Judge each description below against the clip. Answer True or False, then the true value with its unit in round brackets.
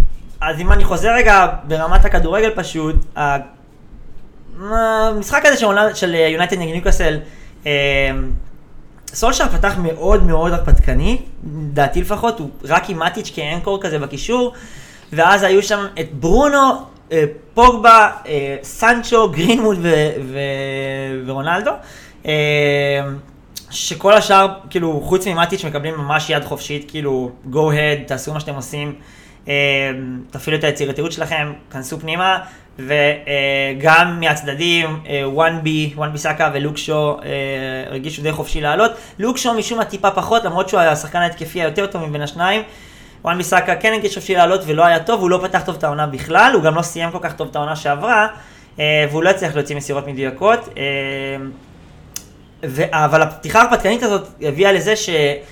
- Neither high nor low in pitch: True (155 Hz)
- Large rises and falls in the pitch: False (5.0 semitones)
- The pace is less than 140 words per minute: False (145 wpm)